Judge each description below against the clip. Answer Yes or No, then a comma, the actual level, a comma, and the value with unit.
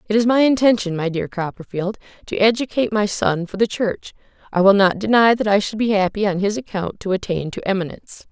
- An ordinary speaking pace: No, fast, 215 wpm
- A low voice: No, high, 205 Hz